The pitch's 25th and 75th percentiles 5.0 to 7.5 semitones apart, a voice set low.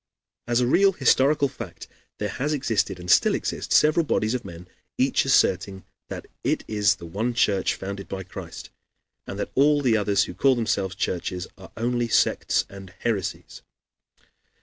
Yes: average, 5.3 semitones; low, 110 Hz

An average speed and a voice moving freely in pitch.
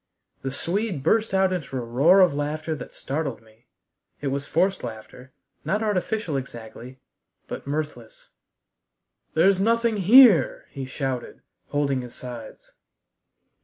No: slow, 130 wpm; wide, 6.8 semitones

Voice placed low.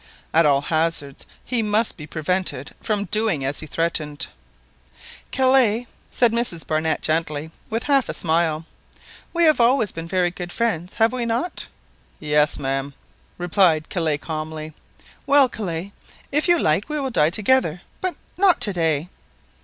No: medium, 175 Hz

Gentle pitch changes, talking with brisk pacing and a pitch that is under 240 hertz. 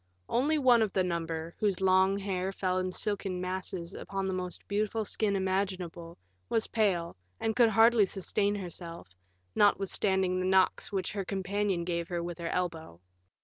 No: narrow, 2.2 semitones; average, 160 wpm; high, 190 Hz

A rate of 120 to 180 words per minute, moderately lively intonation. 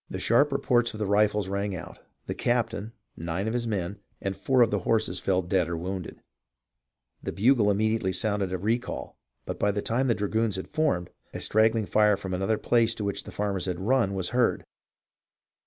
No: average, 195 wpm; average, 3.2 semitones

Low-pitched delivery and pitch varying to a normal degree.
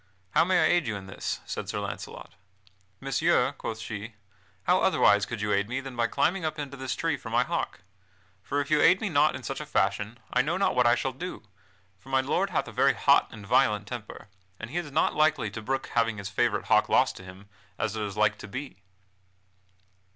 No: low, 125 Hz; wide, 6.0 semitones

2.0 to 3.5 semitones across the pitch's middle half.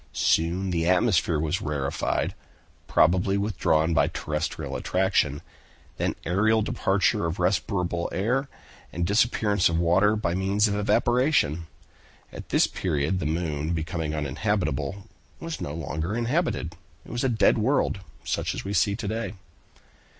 No: average, 4.6 semitones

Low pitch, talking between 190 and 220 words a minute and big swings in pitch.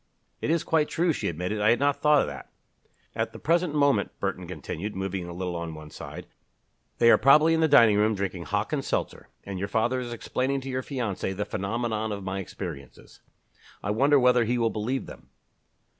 Yes: low, 115 Hz; fast, 205 wpm; wide, 6.0 semitones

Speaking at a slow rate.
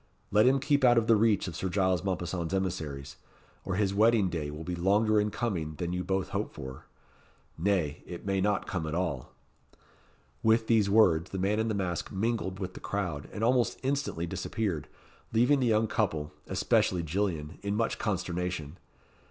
No: average, 180 wpm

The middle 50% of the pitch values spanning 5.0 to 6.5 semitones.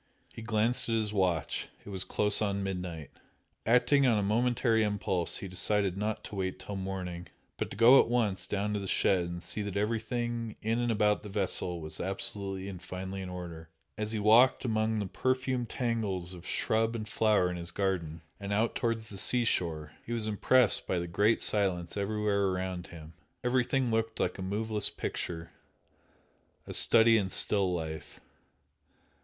No: average, 3.4 semitones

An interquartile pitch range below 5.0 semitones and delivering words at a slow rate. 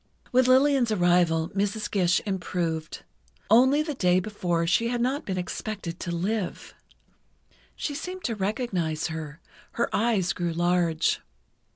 No: wide, 5.5 semitones; slow, 130 wpm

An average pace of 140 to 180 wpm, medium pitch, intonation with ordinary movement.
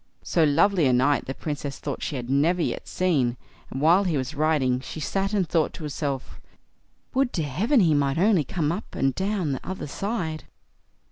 No: average, 195 wpm; medium, 155 Hz; average, 5.0 semitones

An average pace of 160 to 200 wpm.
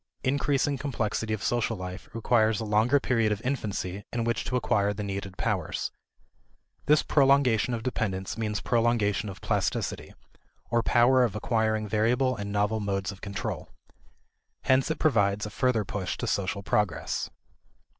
No: average, 150 wpm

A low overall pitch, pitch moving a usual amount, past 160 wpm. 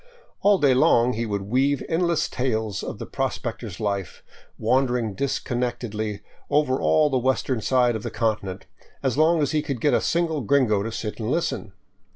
Yes: low, 125 Hz; average, 4.5 semitones; average, 175 wpm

